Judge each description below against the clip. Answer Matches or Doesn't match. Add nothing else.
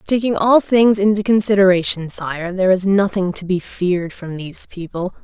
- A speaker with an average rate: Matches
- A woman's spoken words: Matches